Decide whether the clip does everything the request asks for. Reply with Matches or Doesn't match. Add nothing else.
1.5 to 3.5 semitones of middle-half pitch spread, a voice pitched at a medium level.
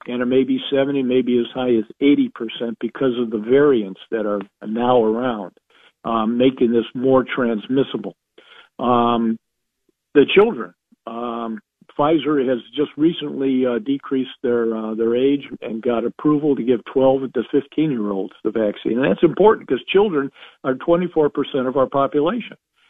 Doesn't match